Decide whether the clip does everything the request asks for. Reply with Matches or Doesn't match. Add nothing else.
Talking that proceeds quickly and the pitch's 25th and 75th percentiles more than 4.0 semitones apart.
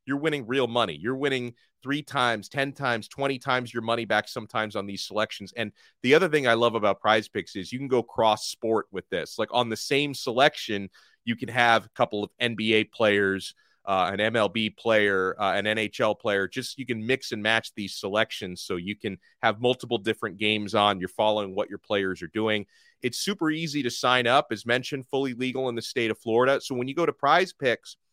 Doesn't match